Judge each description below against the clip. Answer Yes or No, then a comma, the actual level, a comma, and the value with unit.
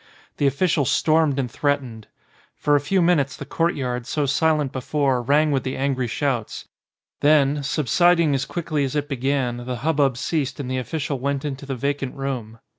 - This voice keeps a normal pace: Yes, average, 180 wpm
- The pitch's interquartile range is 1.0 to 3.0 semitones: Yes, narrow, 2.4 semitones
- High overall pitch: No, medium, 140 Hz